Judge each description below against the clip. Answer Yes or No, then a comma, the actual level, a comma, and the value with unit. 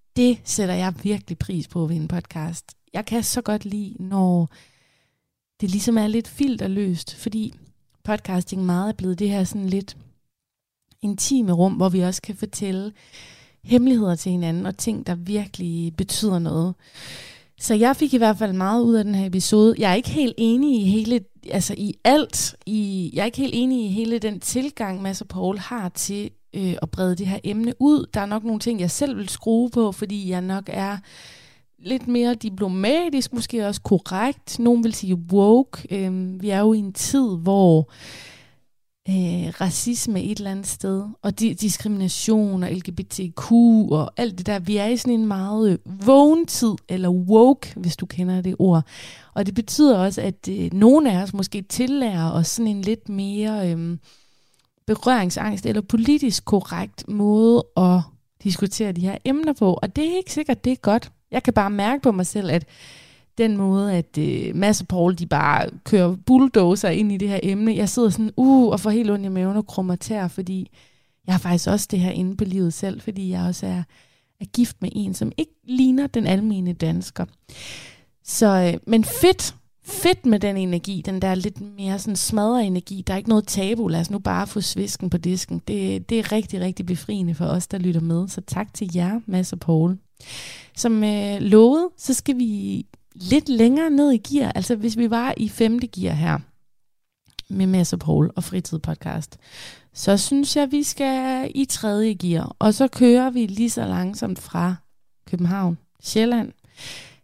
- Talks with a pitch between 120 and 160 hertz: No, high, 200 Hz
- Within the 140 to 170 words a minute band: No, average, 190 wpm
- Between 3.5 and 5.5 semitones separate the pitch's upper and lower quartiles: Yes, average, 3.8 semitones